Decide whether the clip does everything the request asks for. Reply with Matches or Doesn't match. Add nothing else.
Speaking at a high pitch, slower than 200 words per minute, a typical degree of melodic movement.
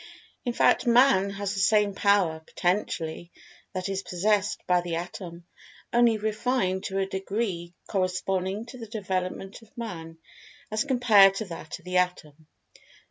Matches